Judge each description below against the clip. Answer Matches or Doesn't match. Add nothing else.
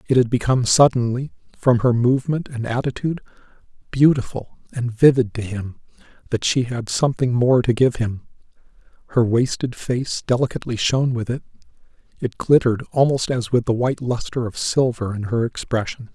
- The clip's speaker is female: Doesn't match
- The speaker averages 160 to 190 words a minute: Doesn't match